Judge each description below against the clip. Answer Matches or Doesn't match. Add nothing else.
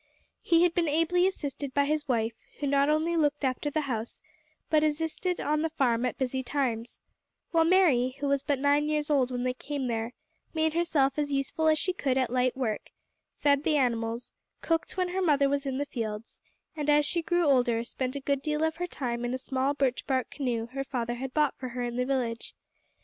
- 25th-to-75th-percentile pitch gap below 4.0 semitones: Matches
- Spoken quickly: Matches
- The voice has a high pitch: Matches